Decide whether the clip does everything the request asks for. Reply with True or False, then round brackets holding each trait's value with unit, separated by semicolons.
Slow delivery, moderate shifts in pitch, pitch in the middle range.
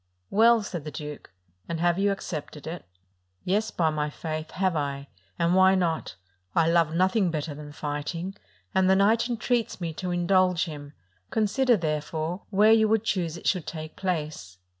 False (175 wpm; 3.9 semitones; 175 Hz)